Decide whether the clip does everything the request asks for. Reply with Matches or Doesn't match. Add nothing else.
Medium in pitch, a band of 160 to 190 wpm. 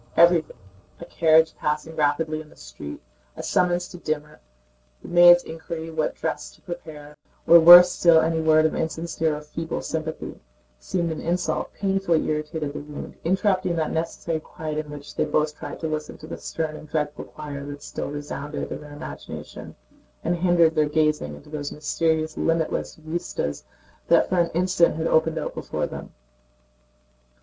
Matches